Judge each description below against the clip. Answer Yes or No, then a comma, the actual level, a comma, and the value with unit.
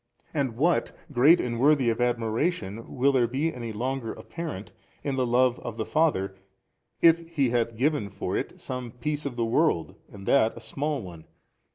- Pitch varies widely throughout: No, average, 4.1 semitones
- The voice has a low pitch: Yes, low, 125 Hz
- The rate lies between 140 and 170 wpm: No, average, 180 wpm